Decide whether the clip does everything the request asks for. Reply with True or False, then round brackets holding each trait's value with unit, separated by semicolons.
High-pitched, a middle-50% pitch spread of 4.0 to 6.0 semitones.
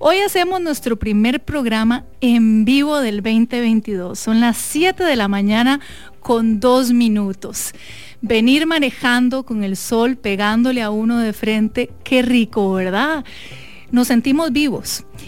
False (235 Hz; 3.3 semitones)